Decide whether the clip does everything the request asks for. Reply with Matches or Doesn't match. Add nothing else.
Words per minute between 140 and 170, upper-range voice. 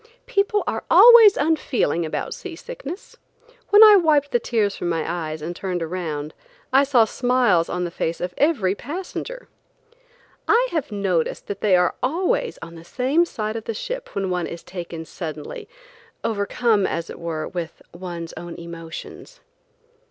Matches